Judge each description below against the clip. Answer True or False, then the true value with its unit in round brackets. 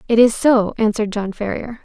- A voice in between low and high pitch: False (220 Hz)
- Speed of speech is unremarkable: True (195 wpm)